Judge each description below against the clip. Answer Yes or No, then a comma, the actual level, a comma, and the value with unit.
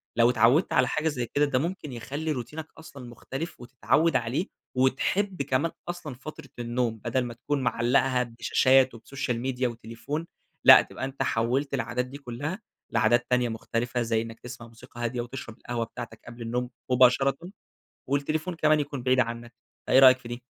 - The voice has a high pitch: No, low, 125 Hz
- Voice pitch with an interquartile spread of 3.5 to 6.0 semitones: No, average, 2.9 semitones